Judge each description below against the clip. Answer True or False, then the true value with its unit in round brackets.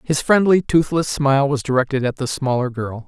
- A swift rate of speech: False (195 wpm)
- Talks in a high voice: False (140 Hz)